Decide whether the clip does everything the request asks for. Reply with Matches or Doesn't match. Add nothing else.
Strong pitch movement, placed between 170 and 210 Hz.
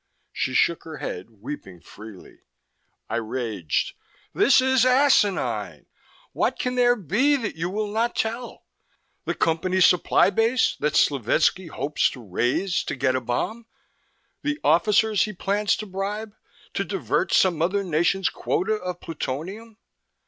Matches